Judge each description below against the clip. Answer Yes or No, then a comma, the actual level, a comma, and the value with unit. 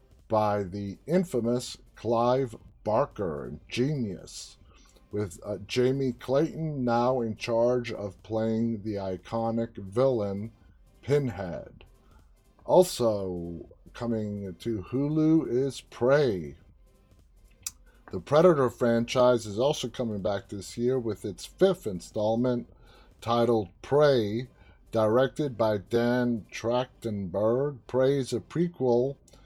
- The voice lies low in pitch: Yes, low, 115 Hz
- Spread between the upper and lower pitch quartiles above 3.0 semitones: Yes, average, 3.6 semitones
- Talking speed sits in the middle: No, slow, 100 wpm